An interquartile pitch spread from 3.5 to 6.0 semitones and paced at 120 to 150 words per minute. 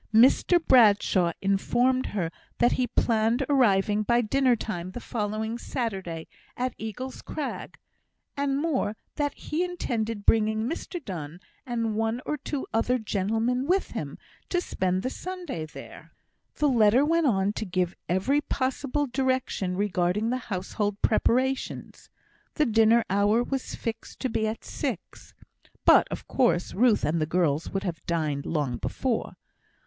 Yes: average, 5.0 semitones; average, 145 wpm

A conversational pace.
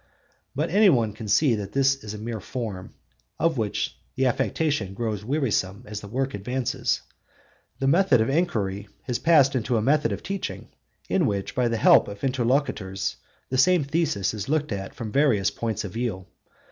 Yes: average, 180 wpm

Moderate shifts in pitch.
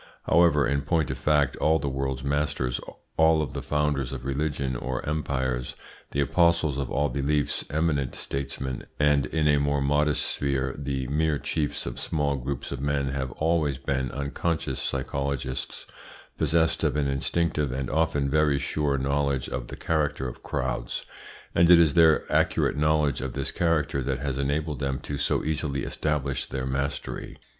No: narrow, 2.1 semitones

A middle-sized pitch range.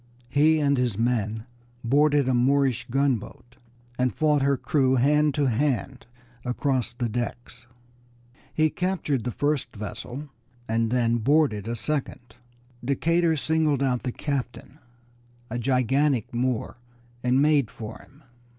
Yes: average, 3.3 semitones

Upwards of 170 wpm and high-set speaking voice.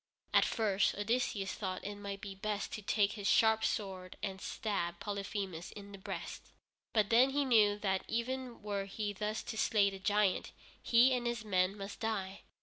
Yes: average, 180 wpm; high, 205 Hz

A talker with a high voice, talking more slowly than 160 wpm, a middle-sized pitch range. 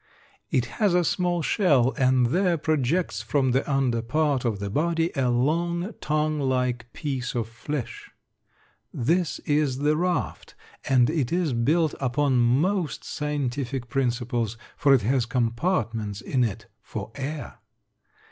No: low, 135 Hz; average, 140 wpm; average, 4.5 semitones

